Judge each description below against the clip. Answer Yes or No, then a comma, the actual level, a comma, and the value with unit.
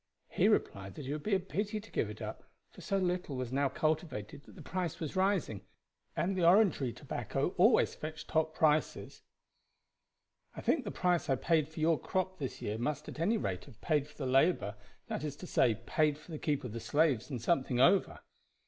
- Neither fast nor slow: No, fast, 210 wpm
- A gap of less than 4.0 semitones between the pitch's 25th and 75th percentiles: No, average, 5.1 semitones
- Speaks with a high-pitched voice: No, medium, 155 Hz